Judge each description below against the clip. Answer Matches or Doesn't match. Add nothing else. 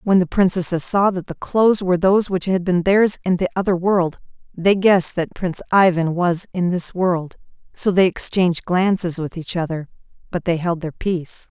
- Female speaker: Matches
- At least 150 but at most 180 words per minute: Doesn't match